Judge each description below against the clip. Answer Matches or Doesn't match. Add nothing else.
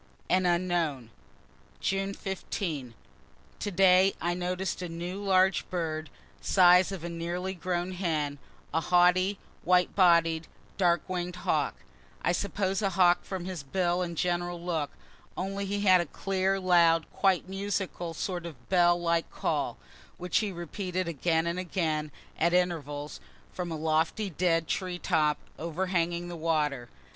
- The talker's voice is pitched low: Doesn't match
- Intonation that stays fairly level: Matches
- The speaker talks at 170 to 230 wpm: Doesn't match